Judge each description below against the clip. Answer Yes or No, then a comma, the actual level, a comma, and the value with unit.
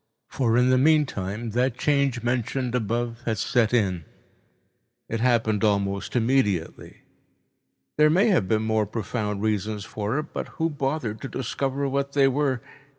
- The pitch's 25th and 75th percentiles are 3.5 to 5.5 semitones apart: Yes, average, 3.9 semitones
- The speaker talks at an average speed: Yes, average, 150 wpm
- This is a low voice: Yes, low, 120 Hz